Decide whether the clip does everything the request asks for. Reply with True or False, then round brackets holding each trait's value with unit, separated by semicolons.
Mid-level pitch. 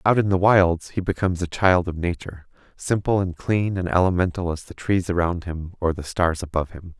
False (90 Hz)